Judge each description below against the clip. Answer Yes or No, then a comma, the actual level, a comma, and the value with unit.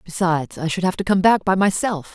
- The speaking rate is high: Yes, fast, 250 wpm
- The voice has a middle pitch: Yes, medium, 180 Hz